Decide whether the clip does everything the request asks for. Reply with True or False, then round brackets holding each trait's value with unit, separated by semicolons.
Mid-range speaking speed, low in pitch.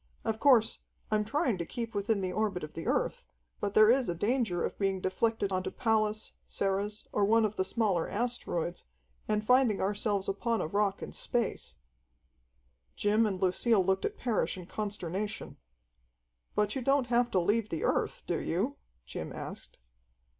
False (170 wpm; 210 Hz)